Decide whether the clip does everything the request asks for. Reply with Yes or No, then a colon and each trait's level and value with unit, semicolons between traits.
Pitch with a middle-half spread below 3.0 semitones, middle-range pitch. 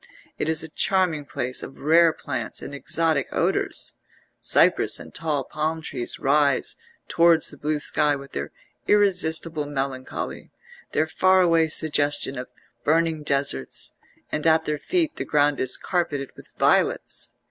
Yes: narrow, 2.6 semitones; medium, 150 Hz